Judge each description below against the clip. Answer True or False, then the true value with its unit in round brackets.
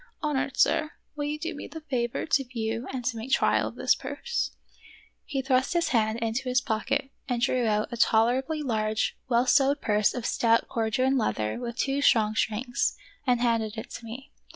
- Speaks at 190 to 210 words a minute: True (200 wpm)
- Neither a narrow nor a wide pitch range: True (3.3 semitones)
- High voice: True (245 Hz)